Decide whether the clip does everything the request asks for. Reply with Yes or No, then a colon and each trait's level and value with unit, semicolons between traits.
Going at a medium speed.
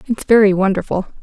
Yes: average, 145 wpm